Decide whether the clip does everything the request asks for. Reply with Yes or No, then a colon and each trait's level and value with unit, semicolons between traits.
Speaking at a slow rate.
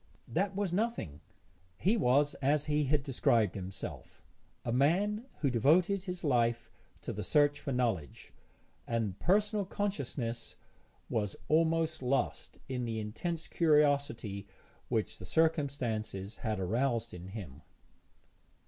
Yes: slow, 120 wpm